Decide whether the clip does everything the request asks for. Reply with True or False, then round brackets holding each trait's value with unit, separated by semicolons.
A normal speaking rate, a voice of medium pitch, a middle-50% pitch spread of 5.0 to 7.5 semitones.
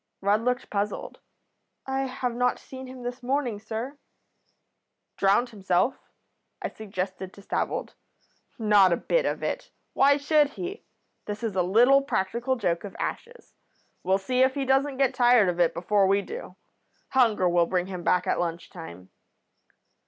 False (160 wpm; 225 Hz; 5.6 semitones)